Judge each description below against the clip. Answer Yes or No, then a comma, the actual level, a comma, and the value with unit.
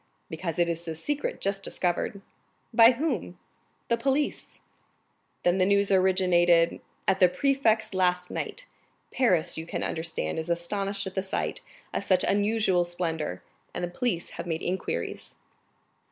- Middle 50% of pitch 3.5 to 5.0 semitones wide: No, average, 3.0 semitones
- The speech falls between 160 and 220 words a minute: No, average, 145 wpm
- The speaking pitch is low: No, medium, 185 Hz